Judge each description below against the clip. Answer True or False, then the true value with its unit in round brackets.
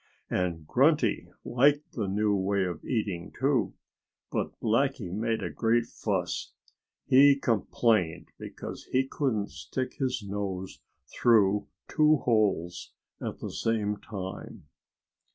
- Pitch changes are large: False (4.5 semitones)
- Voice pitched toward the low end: True (110 Hz)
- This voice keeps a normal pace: False (115 wpm)